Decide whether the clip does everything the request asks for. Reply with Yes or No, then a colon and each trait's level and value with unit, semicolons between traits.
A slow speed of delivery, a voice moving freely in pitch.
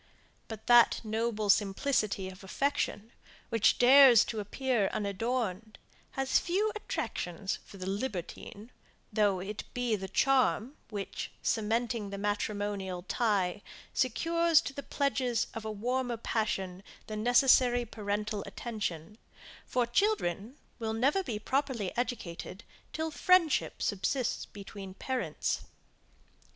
No: slow, 115 wpm; average, 4.0 semitones